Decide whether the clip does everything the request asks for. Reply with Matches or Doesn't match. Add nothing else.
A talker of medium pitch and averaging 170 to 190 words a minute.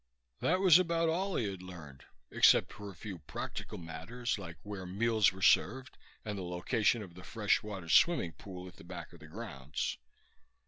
Doesn't match